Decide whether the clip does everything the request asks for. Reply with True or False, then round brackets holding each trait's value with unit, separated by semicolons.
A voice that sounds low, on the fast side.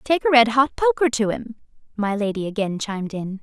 False (225 Hz; 210 wpm)